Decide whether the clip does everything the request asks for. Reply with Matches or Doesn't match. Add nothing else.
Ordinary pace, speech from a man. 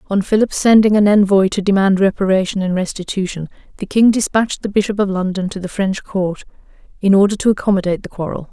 Doesn't match